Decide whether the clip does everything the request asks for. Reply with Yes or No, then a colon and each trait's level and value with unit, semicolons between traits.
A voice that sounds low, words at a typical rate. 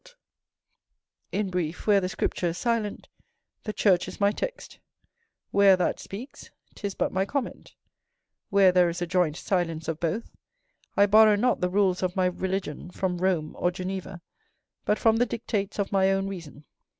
No: high, 190 Hz; average, 165 wpm